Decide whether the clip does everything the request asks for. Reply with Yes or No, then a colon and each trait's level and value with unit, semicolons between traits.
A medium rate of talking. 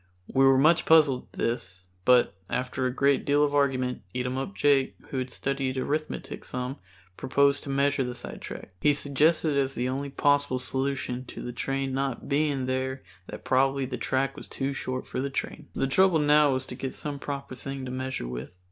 Yes: average, 190 wpm